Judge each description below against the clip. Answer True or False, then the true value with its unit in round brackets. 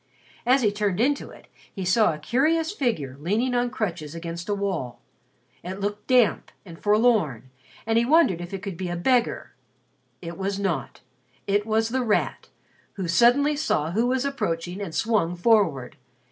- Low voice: False (205 Hz)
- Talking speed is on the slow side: False (170 wpm)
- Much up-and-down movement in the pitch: True (5.8 semitones)